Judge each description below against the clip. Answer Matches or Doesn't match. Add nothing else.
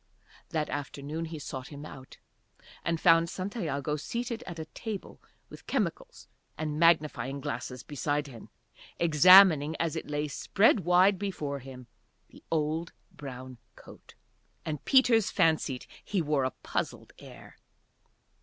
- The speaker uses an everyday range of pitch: Matches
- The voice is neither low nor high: Matches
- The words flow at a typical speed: Doesn't match